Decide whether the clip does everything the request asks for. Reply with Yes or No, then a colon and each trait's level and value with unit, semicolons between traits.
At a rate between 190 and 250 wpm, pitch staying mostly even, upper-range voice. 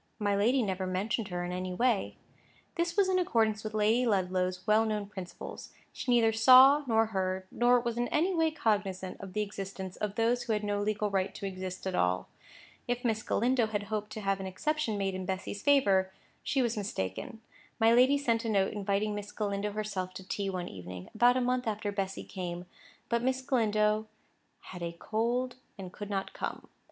No: average, 195 wpm; average, 3.8 semitones; high, 210 Hz